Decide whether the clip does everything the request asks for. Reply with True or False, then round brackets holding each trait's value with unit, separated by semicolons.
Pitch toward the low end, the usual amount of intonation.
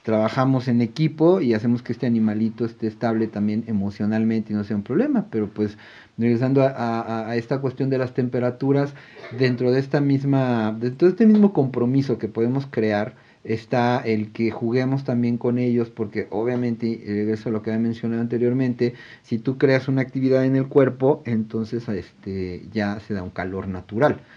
True (120 Hz; 3.0 semitones)